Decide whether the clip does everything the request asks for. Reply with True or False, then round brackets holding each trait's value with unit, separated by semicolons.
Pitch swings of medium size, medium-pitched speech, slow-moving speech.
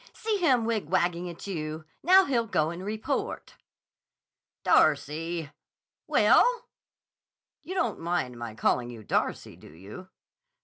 False (7.3 semitones; 175 Hz; 120 wpm)